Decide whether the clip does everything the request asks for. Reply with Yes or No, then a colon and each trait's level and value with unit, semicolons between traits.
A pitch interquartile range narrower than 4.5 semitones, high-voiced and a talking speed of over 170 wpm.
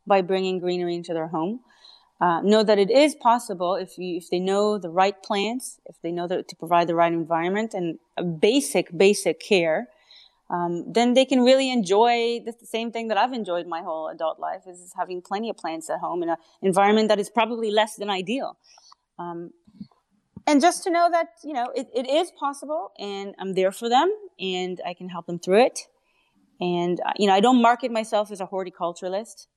No: average, 4.8 semitones; high, 200 Hz; average, 200 wpm